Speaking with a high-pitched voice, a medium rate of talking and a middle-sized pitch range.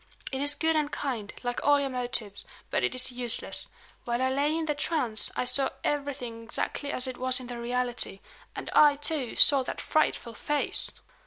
Yes: very high, 255 Hz; average, 190 wpm; average, 3.0 semitones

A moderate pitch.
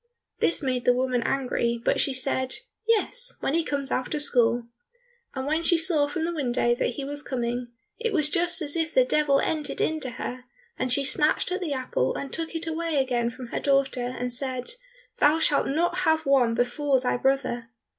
No: very high, 275 Hz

